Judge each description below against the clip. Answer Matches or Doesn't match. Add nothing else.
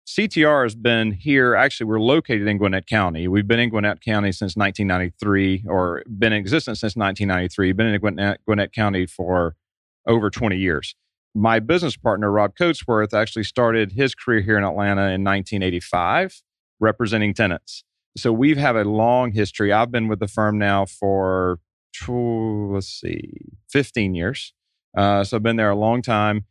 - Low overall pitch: Matches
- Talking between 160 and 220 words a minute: Matches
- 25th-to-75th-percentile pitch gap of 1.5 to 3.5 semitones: Matches